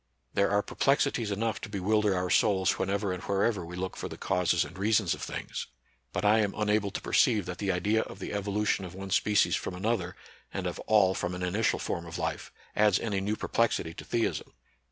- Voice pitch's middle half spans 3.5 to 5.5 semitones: No, narrow, 2.6 semitones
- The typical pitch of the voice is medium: No, low, 100 Hz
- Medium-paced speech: No, fast, 215 wpm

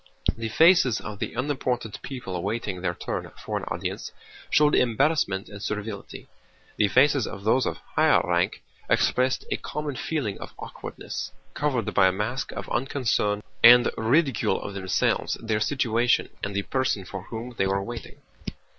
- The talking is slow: No, average, 155 wpm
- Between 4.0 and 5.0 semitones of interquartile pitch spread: Yes, average, 4.5 semitones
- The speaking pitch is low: Yes, low, 115 Hz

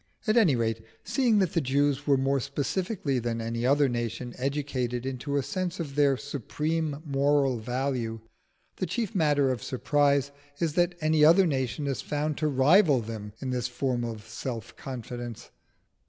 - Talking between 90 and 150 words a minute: No, average, 165 wpm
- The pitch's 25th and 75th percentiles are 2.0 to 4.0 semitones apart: Yes, average, 3.7 semitones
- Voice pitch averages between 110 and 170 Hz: Yes, medium, 140 Hz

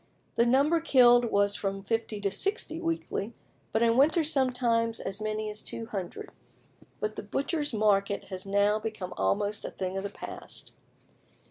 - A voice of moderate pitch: No, high, 220 Hz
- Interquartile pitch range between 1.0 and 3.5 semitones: No, average, 4.2 semitones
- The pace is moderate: Yes, average, 155 wpm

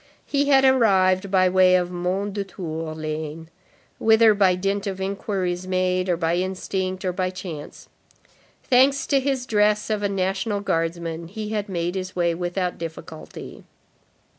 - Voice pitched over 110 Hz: Yes, medium, 185 Hz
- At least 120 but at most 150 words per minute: Yes, average, 140 wpm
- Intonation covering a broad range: No, average, 2.7 semitones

